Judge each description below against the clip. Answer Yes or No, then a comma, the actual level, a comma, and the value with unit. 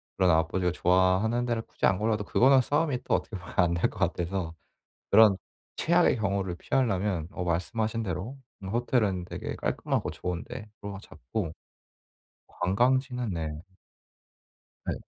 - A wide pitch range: No, average, 4.4 semitones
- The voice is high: No, very low, 95 Hz